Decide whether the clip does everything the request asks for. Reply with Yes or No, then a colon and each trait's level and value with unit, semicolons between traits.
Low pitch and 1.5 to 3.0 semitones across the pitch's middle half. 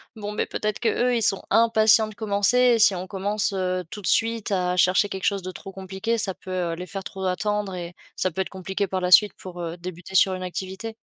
No: high, 190 Hz; narrow, 2.4 semitones